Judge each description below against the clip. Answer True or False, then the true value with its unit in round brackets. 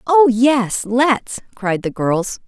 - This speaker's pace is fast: False (145 wpm)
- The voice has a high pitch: True (235 Hz)